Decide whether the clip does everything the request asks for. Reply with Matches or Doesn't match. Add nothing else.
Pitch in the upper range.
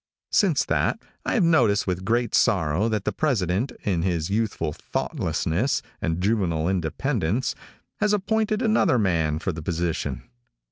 Doesn't match